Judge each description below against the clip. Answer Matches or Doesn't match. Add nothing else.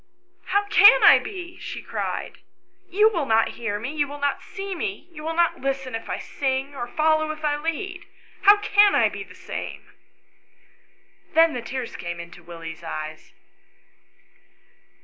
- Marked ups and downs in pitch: Matches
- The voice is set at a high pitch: Matches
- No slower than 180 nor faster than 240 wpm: Doesn't match